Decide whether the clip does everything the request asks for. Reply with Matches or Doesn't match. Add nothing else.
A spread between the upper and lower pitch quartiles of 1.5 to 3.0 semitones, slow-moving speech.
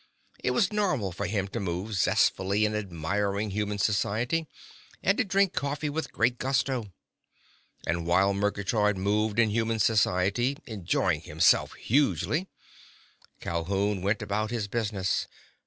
Doesn't match